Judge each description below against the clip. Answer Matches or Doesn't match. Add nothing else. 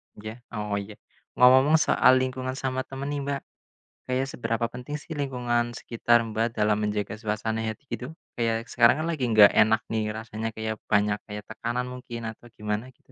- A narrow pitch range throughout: Doesn't match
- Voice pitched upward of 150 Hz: Doesn't match